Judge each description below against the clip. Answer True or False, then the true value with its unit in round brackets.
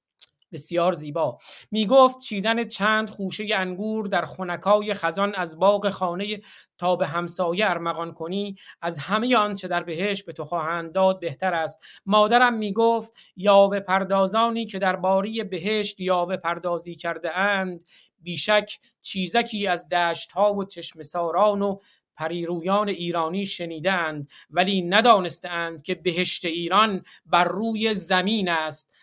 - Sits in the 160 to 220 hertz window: True (185 Hz)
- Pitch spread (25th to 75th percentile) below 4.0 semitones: True (3.2 semitones)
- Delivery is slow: False (130 wpm)